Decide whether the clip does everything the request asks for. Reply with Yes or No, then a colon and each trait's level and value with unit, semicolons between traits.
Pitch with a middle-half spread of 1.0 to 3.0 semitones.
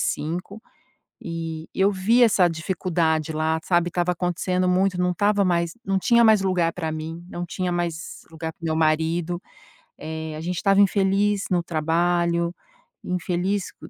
Yes: narrow, 2.5 semitones